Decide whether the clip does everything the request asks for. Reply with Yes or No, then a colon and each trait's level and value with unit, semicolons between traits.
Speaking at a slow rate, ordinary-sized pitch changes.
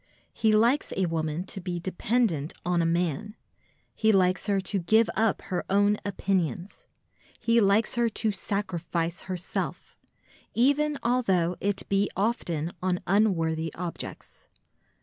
Yes: slow, 130 wpm; average, 4.0 semitones